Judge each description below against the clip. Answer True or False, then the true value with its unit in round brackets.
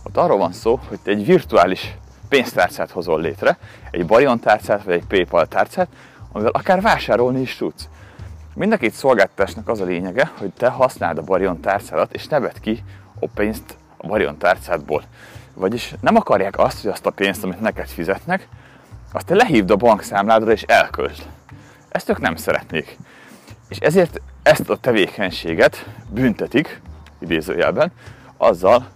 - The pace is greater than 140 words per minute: True (155 wpm)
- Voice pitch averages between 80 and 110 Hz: True (100 Hz)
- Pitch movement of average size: True (4.5 semitones)